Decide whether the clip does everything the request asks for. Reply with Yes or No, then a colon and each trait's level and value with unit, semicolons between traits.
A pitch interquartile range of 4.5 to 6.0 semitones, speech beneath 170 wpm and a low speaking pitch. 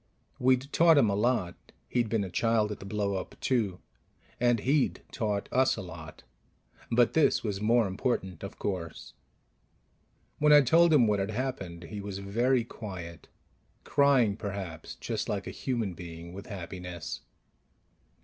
Yes: average, 4.8 semitones; average, 155 wpm; low, 105 Hz